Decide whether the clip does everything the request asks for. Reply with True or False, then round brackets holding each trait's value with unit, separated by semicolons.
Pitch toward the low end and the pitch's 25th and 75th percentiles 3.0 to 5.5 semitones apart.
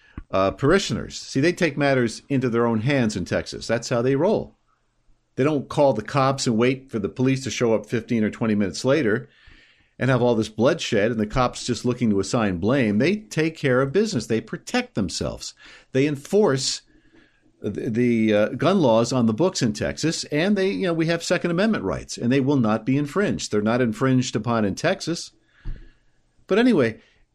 True (125 Hz; 4.6 semitones)